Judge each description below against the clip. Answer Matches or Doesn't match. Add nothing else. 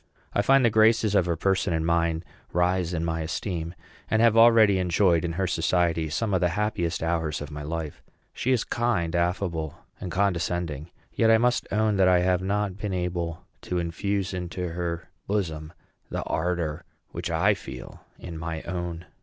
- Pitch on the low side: Matches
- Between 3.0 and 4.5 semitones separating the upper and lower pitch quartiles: Matches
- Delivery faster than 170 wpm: Matches